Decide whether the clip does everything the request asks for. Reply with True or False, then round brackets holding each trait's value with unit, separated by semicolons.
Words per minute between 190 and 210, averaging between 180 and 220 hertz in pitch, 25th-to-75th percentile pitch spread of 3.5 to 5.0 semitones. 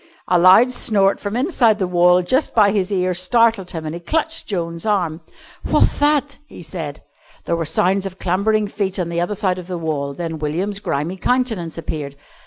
True (195 wpm; 185 Hz; 3.9 semitones)